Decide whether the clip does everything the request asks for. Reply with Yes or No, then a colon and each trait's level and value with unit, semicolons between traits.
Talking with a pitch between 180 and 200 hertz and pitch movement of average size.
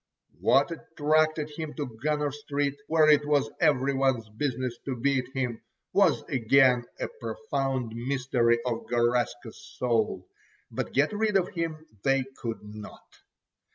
No: low, 135 Hz; average, 3.7 semitones